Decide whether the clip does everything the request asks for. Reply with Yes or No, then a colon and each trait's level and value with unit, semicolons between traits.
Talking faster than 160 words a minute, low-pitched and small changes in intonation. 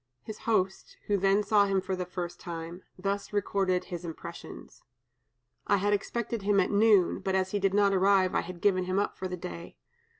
No: average, 200 wpm; high, 195 Hz; narrow, 1.8 semitones